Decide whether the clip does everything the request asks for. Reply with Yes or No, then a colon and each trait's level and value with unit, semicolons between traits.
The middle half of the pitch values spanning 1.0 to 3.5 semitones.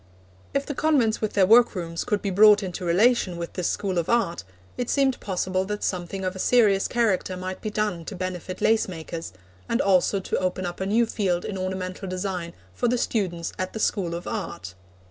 Yes: average, 3.1 semitones